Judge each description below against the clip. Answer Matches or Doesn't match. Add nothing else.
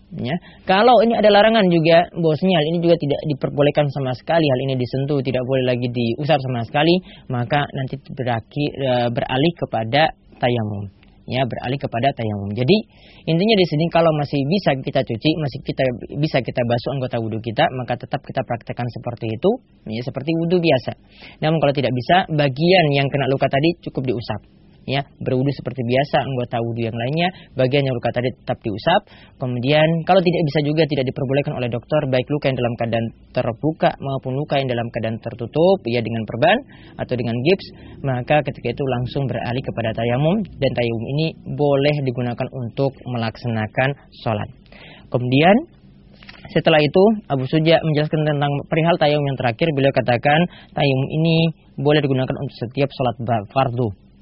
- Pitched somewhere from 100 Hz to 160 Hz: Matches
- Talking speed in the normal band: Doesn't match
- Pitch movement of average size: Matches